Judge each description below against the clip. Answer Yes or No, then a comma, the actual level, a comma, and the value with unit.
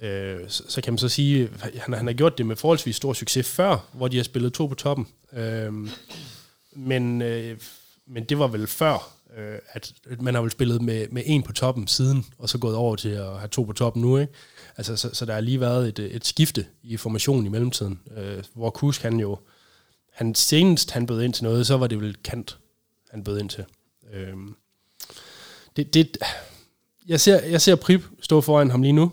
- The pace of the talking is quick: No, average, 200 wpm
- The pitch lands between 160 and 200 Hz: No, low, 120 Hz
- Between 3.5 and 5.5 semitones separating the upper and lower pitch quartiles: Yes, average, 3.8 semitones